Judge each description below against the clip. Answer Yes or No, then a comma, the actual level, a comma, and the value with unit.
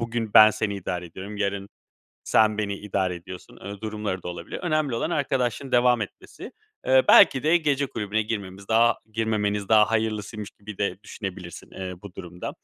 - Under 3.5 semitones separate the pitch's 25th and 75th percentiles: Yes, average, 2.7 semitones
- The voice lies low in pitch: Yes, low, 105 Hz